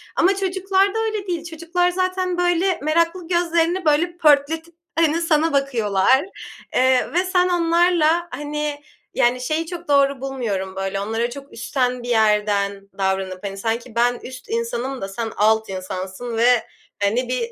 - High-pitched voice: Yes, very high, 280 Hz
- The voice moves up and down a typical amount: No, wide, 7.1 semitones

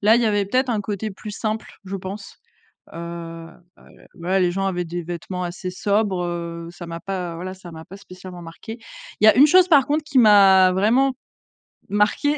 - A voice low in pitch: No, high, 190 Hz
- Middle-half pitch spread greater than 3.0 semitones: Yes, average, 3.6 semitones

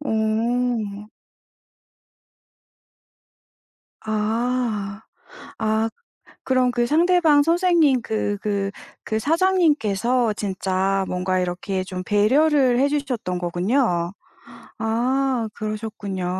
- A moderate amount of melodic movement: Yes, average, 4.8 semitones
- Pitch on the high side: Yes, high, 220 Hz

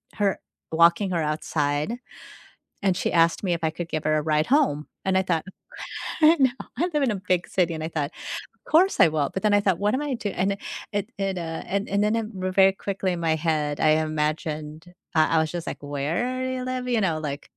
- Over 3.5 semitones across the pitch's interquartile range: Yes, average, 4.5 semitones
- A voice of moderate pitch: Yes, medium, 175 Hz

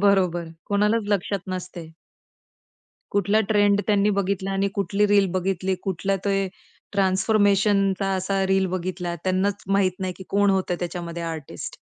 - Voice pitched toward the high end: Yes, high, 195 Hz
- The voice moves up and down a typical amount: No, narrow, 1.5 semitones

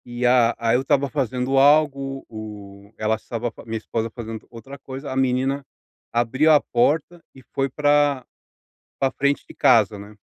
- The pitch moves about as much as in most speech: Yes, average, 3.3 semitones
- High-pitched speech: No, low, 130 Hz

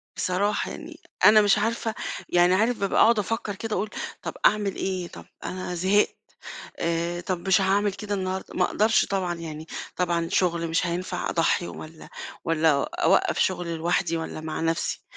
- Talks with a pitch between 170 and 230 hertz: Yes, medium, 185 Hz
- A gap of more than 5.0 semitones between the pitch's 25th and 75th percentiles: No, average, 3.3 semitones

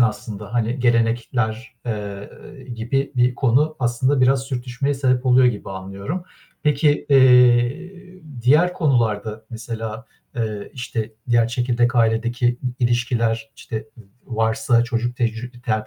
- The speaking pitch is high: No, low, 120 Hz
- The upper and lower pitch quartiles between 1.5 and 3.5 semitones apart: Yes, narrow, 2.5 semitones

